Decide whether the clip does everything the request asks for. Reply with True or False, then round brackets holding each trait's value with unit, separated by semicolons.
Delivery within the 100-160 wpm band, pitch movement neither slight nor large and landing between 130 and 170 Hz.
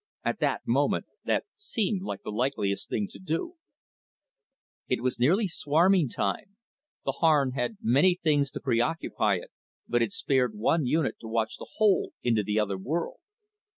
False (155 wpm; 7.0 semitones; 135 Hz)